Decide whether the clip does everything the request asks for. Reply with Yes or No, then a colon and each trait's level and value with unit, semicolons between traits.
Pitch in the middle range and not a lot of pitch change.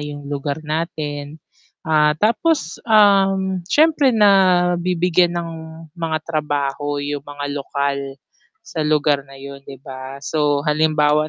No: medium, 155 Hz; average, 3.6 semitones